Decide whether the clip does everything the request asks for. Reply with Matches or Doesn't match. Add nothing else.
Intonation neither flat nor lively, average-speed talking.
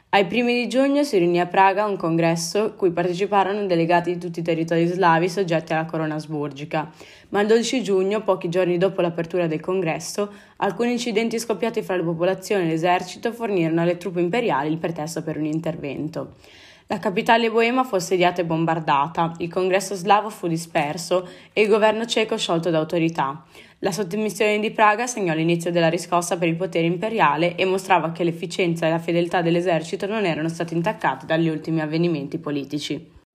Doesn't match